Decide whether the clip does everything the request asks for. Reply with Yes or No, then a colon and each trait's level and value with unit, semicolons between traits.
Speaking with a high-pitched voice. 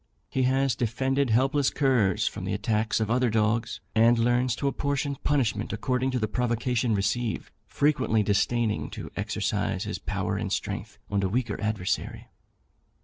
No: low, 120 Hz